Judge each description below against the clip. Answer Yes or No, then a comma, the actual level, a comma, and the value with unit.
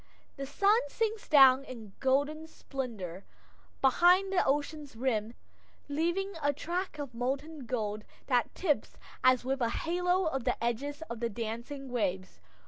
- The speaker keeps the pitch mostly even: No, average, 5.1 semitones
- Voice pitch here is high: Yes, very high, 275 Hz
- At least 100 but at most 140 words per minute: Yes, slow, 135 wpm